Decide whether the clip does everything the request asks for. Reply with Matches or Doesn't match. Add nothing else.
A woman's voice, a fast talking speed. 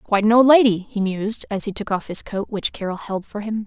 Matches